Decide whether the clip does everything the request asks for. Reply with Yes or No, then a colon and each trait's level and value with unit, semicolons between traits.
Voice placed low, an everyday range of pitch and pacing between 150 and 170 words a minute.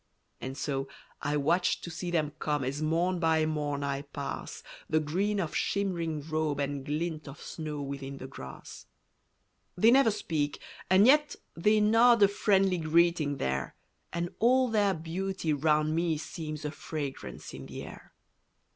No: medium, 155 Hz; average, 4.3 semitones; average, 155 wpm